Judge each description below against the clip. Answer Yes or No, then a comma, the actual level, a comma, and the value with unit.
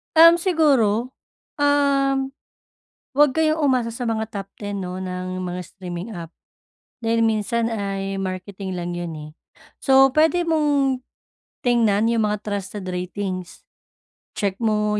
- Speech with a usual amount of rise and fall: No, wide, 6.1 semitones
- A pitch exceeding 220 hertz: No, high, 215 Hz